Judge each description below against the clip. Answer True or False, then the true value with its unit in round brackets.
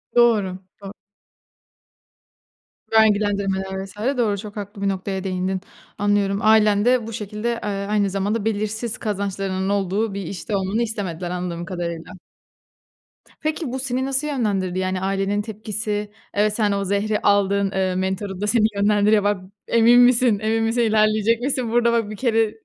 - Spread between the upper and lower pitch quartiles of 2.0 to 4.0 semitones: True (2.4 semitones)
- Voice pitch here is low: False (205 Hz)